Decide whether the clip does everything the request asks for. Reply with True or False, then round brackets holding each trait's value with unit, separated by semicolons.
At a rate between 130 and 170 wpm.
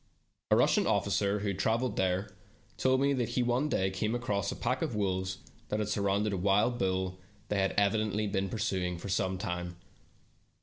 False (185 wpm)